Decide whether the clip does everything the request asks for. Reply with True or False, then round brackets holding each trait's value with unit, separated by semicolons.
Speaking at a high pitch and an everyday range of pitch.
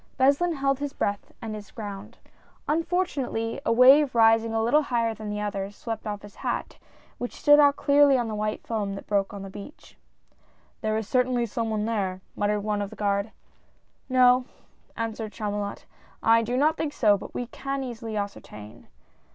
True (225 Hz; 3.9 semitones)